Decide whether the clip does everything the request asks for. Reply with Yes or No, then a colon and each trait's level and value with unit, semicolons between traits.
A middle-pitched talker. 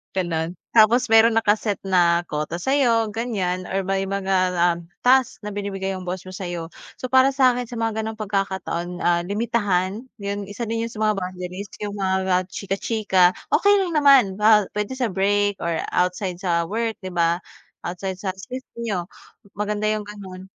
No: high, 200 Hz